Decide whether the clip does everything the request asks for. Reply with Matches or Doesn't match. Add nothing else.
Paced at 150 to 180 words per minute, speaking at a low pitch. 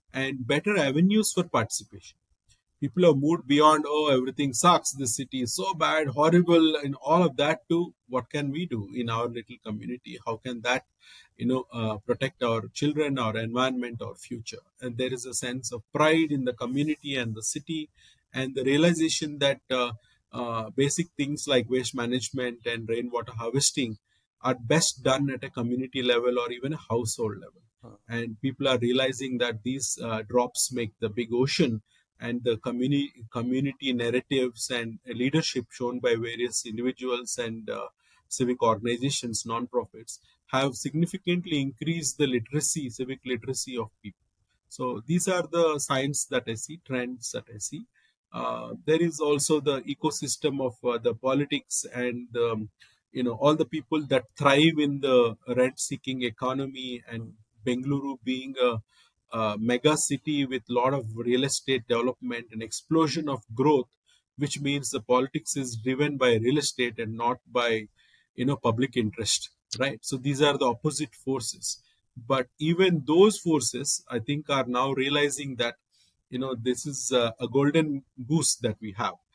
Matches